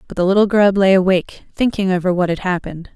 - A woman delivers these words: Yes, female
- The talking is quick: Yes, fast, 225 wpm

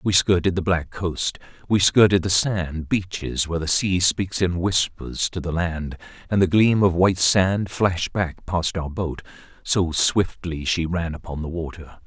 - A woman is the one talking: No, male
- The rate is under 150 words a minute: No, average, 185 wpm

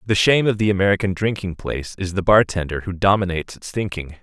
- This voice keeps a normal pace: No, fast, 215 wpm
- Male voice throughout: Yes, male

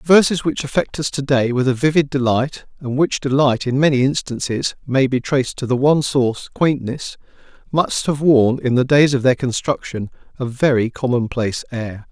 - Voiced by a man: Yes, male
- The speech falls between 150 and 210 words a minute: Yes, average, 185 wpm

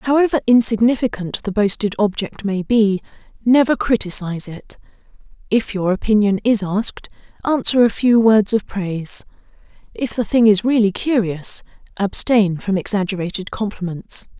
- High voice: Yes, high, 210 Hz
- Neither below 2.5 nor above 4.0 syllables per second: No, 4.9 syllables/s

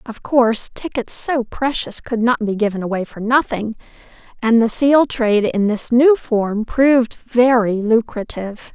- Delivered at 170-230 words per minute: No, average, 160 wpm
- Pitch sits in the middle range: No, high, 230 Hz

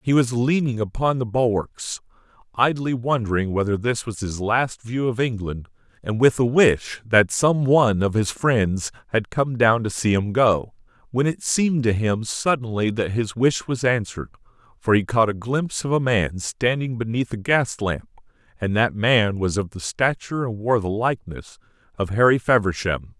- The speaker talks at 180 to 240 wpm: Yes, average, 185 wpm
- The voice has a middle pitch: No, low, 115 Hz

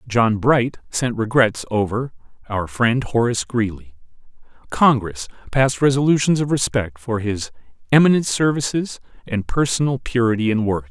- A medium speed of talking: No, slow, 125 wpm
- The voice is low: Yes, low, 120 Hz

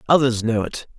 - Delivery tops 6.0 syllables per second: No, 5.5 syllables/s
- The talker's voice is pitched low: Yes, low, 120 Hz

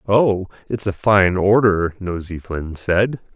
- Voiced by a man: Yes, male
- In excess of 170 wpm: No, average, 145 wpm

